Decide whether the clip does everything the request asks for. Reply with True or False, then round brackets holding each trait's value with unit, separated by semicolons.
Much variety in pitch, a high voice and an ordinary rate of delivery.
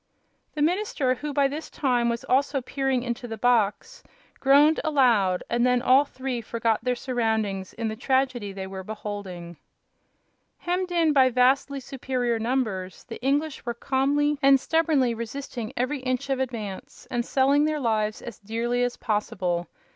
False (3.7 semitones; 250 Hz; 155 wpm)